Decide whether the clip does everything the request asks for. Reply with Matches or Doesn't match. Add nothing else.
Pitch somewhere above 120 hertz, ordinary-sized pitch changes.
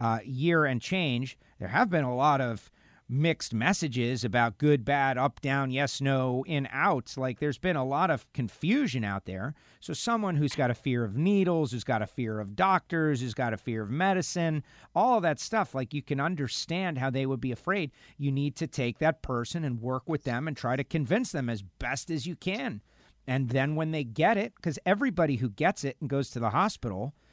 Matches